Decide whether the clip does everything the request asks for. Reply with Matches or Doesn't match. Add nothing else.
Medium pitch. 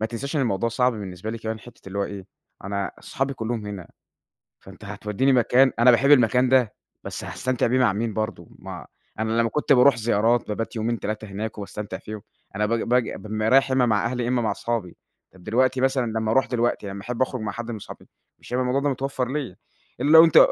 Doesn't match